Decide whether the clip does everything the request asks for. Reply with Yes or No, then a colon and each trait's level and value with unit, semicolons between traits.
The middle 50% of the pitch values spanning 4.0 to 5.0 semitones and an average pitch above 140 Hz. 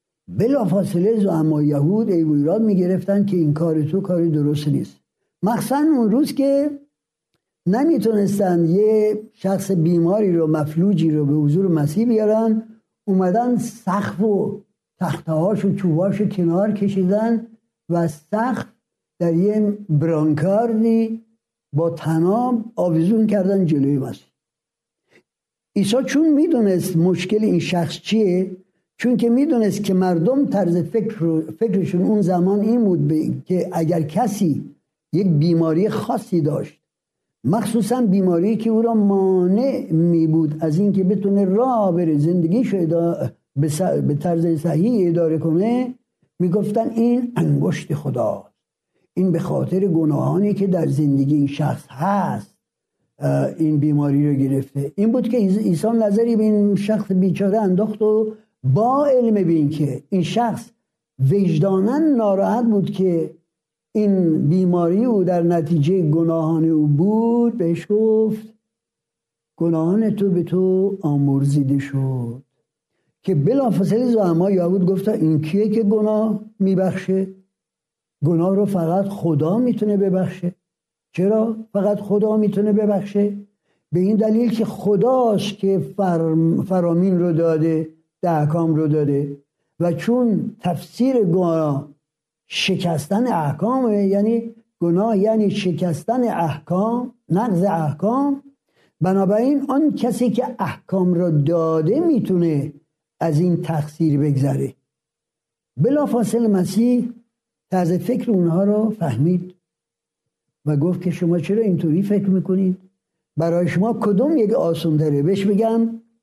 Yes: average, 4.7 semitones; high, 190 Hz